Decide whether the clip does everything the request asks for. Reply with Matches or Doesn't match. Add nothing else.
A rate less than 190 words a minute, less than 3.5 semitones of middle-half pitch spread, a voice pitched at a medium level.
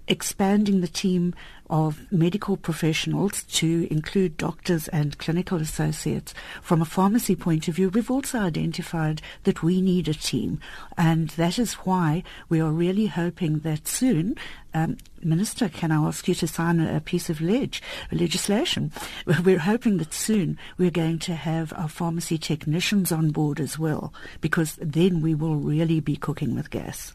Matches